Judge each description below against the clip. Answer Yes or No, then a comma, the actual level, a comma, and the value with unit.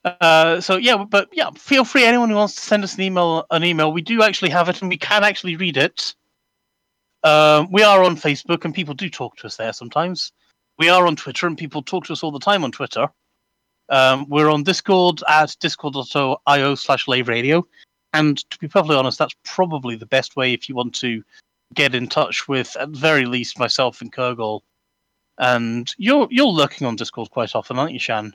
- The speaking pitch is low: No, medium, 155 Hz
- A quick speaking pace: Yes, fast, 210 wpm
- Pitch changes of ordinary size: No, wide, 6.0 semitones